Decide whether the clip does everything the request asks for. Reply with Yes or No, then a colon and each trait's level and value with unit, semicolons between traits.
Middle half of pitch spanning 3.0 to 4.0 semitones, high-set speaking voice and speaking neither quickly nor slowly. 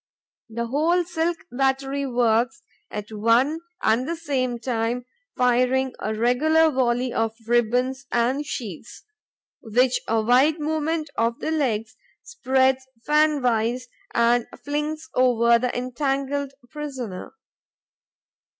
No: average, 3.5 semitones; very high, 255 Hz; slow, 115 wpm